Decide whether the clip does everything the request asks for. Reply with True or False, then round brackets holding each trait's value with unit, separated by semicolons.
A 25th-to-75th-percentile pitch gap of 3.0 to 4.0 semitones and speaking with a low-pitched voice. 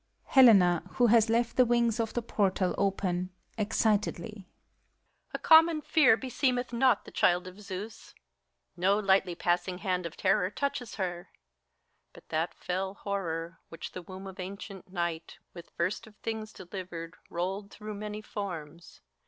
False (3.7 semitones; 195 Hz)